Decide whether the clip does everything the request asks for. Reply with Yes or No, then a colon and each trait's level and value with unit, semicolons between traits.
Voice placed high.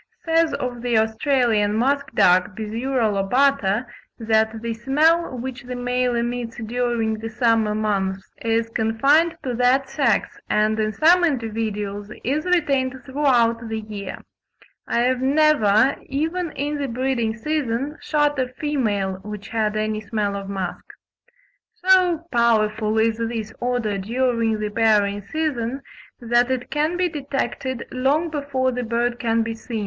Yes: high, 235 Hz